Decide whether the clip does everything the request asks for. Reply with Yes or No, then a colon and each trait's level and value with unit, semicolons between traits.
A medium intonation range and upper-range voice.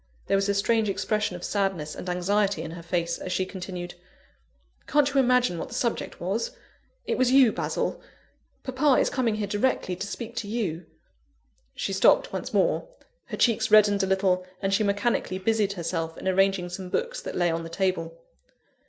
Yes: average, 4.0 semitones; high, 195 Hz